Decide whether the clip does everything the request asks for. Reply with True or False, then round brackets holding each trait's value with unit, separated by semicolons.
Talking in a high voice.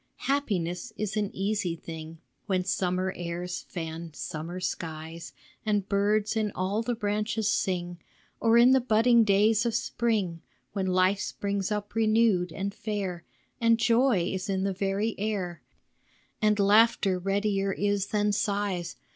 True (200 Hz)